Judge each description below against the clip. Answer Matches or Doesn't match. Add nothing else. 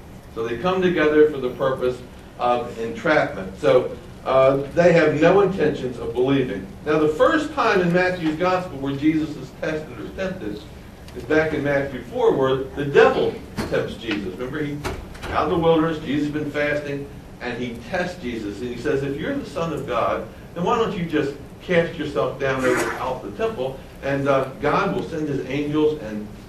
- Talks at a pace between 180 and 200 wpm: Matches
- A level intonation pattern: Doesn't match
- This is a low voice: Doesn't match